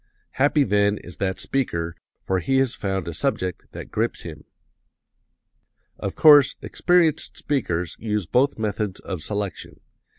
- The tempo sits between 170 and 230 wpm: No, slow, 135 wpm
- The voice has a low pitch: Yes, low, 105 Hz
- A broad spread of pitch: Yes, wide, 6.4 semitones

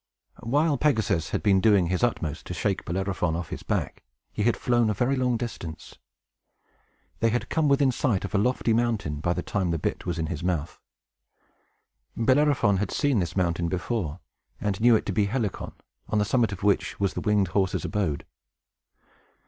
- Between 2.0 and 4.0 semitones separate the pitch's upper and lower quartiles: No, average, 5.0 semitones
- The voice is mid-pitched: No, low, 105 Hz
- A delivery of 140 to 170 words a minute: No, average, 190 wpm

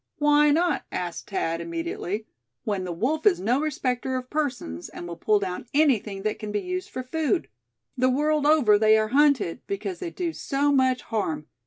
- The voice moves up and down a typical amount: No, wide, 6.6 semitones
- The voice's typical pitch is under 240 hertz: No, very high, 255 Hz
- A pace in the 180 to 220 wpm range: Yes, average, 185 wpm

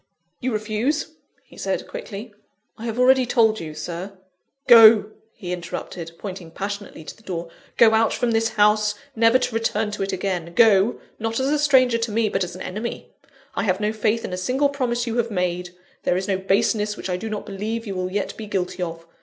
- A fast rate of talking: Yes, fast, 210 wpm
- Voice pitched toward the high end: Yes, high, 215 Hz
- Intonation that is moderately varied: Yes, average, 3.6 semitones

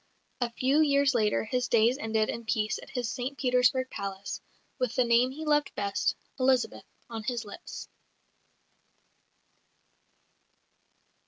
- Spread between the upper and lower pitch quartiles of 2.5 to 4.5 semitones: Yes, average, 2.8 semitones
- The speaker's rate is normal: No, slow, 130 wpm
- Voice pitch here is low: No, high, 245 Hz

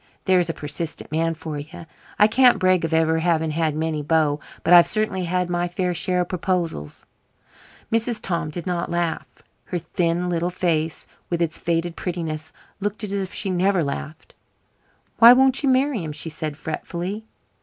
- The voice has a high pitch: No, medium, 170 Hz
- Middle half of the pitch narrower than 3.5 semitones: Yes, narrow, 2.4 semitones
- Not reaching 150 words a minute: No, average, 175 wpm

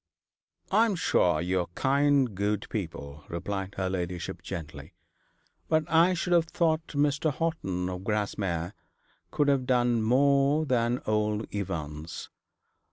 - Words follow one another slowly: Yes, slow, 130 wpm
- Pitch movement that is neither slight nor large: No, wide, 7.9 semitones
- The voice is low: Yes, low, 105 Hz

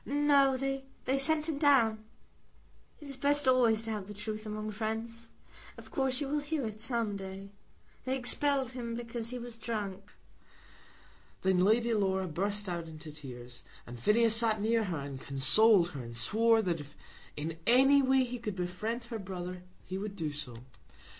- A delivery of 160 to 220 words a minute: Yes, average, 175 wpm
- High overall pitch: Yes, high, 220 Hz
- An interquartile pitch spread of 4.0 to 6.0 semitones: Yes, average, 5.1 semitones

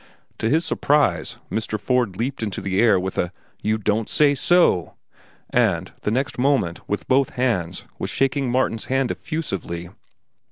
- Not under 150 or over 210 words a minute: Yes, average, 155 wpm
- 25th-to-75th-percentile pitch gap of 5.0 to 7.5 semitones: Yes, wide, 5.4 semitones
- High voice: No, low, 120 Hz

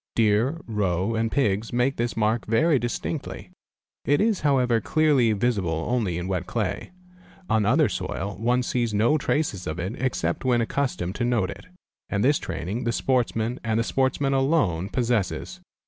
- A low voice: Yes, low, 115 Hz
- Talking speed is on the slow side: No, average, 160 wpm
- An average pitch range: Yes, average, 4.3 semitones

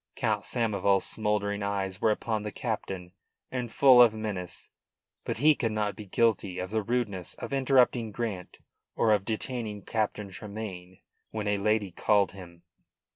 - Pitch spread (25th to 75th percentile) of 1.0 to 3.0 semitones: Yes, narrow, 2.5 semitones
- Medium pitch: No, low, 105 Hz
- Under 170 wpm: Yes, average, 155 wpm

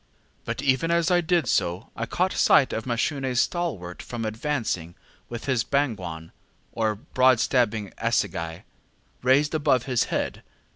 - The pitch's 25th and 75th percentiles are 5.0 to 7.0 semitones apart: Yes, average, 5.3 semitones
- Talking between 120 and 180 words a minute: Yes, average, 140 wpm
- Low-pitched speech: Yes, low, 125 Hz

